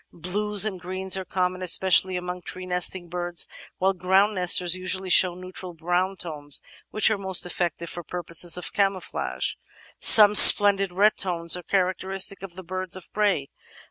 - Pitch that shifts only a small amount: Yes, narrow, 1.6 semitones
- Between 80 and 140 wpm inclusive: No, average, 170 wpm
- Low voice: No, medium, 185 Hz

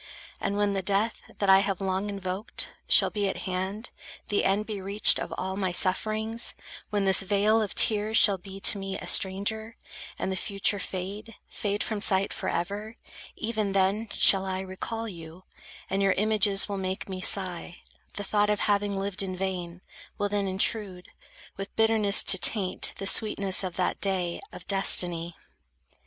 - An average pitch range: No, narrow, 1.7 semitones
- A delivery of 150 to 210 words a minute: Yes, average, 170 wpm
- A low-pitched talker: No, high, 195 Hz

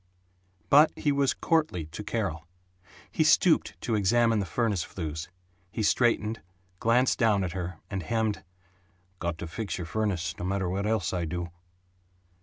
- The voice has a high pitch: No, low, 100 Hz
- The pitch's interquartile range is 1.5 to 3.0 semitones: No, average, 4.7 semitones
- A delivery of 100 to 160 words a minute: Yes, average, 155 wpm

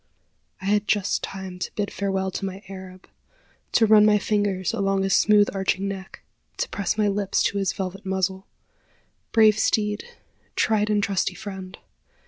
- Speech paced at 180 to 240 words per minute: No, average, 160 wpm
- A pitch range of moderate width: No, narrow, 1.5 semitones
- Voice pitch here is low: No, high, 195 Hz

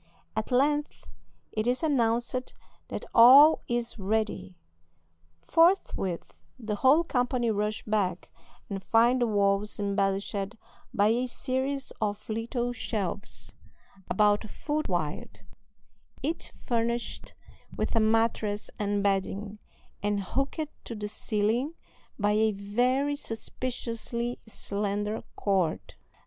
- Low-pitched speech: No, high, 220 Hz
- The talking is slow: Yes, slow, 110 wpm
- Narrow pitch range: No, average, 3.4 semitones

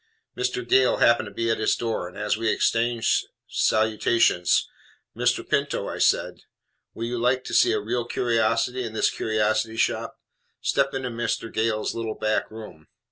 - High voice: No, low, 115 Hz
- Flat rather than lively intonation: Yes, narrow, 1.8 semitones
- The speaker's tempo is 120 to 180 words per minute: Yes, average, 165 wpm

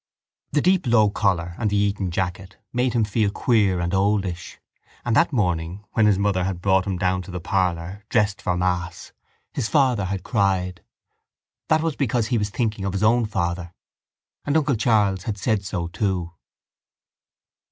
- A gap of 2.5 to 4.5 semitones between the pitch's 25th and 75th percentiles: Yes, average, 3.2 semitones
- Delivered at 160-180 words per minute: Yes, average, 175 wpm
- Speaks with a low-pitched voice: Yes, low, 100 Hz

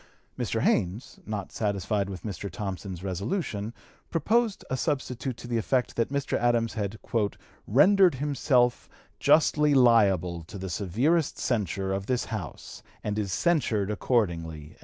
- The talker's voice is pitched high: No, low, 110 Hz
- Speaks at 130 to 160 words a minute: Yes, slow, 135 wpm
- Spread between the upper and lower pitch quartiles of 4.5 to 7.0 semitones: Yes, average, 5.3 semitones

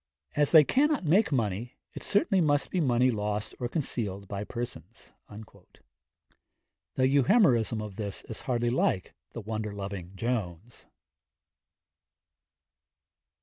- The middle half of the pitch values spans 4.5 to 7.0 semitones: Yes, wide, 5.6 semitones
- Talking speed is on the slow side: Yes, slow, 115 wpm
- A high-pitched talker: No, low, 120 Hz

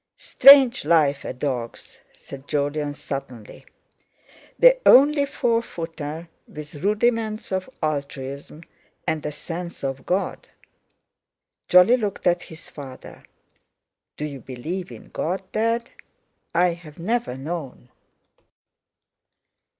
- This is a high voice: No, medium, 165 Hz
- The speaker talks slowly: Yes, slow, 105 wpm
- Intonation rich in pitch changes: Yes, wide, 6.9 semitones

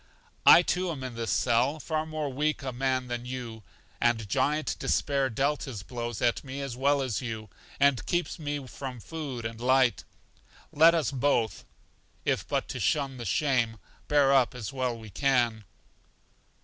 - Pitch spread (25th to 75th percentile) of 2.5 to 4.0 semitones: Yes, average, 3.3 semitones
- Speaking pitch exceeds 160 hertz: No, low, 130 Hz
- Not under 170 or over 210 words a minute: Yes, average, 175 wpm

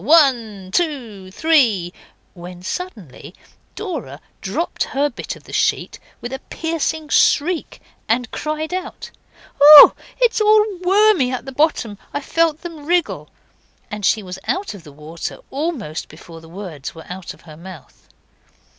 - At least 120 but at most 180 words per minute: Yes, average, 145 wpm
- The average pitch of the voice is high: Yes, very high, 255 Hz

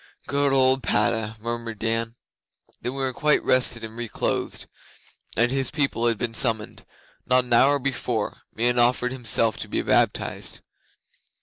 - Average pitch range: No, narrow, 2.3 semitones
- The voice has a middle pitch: No, low, 120 Hz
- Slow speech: No, average, 150 wpm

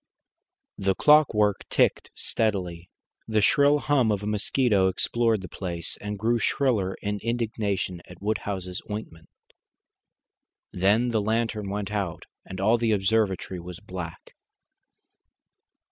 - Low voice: Yes, low, 105 Hz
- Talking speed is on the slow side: Yes, slow, 120 wpm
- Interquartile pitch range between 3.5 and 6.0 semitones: No, average, 3.1 semitones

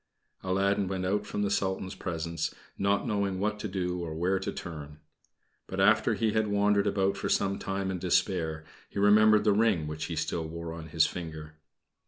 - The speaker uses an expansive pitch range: No, average, 3.4 semitones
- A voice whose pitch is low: Yes, very low, 95 Hz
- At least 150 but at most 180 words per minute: No, average, 190 wpm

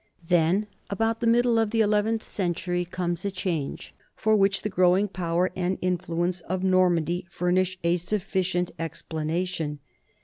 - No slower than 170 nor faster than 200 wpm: No, average, 145 wpm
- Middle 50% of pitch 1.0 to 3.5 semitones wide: Yes, narrow, 2.4 semitones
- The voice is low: No, medium, 185 Hz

